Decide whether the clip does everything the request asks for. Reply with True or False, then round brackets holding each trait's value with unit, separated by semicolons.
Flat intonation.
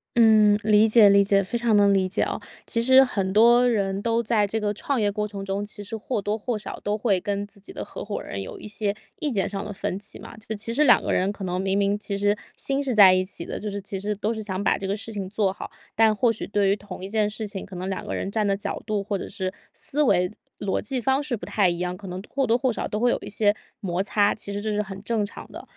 True (2.1 semitones)